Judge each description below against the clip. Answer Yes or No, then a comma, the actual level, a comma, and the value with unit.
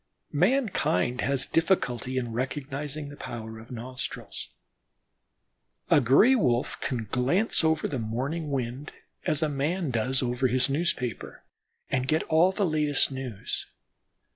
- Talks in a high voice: No, low, 135 Hz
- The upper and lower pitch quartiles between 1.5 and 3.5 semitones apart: No, average, 4.0 semitones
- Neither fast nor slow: No, slow, 130 wpm